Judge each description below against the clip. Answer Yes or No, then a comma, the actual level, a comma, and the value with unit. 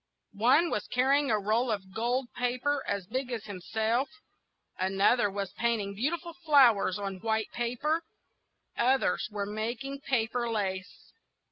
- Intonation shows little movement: No, average, 4.2 semitones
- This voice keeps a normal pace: No, slow, 130 wpm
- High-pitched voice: Yes, high, 230 Hz